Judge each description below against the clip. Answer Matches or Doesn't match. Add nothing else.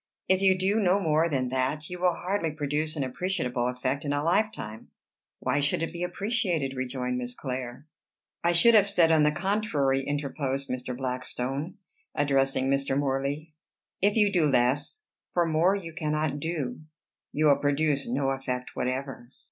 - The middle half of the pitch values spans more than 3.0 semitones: Matches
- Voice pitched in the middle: Matches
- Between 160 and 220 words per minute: Matches